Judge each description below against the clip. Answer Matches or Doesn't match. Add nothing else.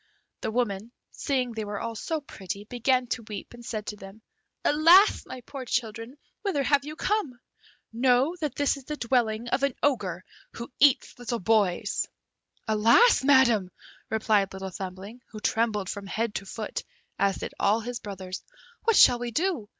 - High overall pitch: Matches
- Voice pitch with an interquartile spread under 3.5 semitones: Doesn't match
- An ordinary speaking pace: Matches